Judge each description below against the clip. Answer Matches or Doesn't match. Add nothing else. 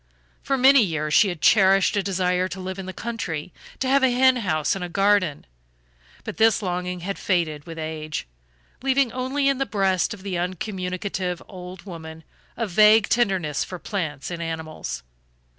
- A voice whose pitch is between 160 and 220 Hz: Matches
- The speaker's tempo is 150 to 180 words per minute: Matches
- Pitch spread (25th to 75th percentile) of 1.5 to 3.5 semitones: Doesn't match